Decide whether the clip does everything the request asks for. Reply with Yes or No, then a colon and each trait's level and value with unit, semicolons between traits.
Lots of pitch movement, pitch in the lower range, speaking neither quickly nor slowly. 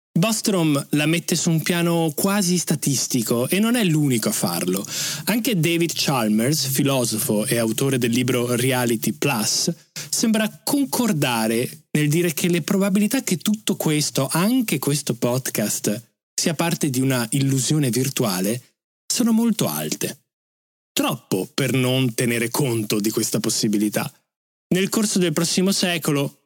No: wide, 6.6 semitones; medium, 150 Hz; average, 135 wpm